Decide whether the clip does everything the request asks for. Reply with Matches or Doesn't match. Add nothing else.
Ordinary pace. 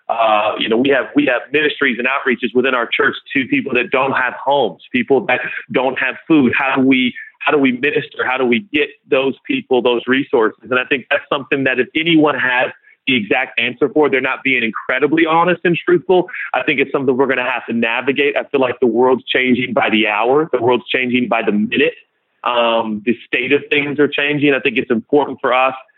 Doesn't match